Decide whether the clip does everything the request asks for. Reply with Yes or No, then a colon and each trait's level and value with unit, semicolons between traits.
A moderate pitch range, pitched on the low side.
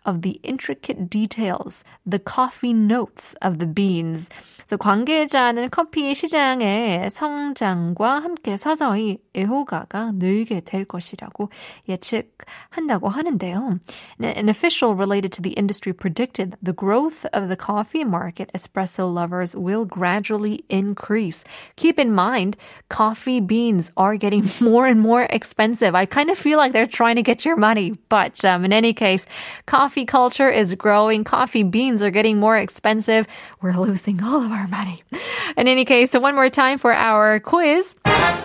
No: average, 4.6 semitones; high, 215 Hz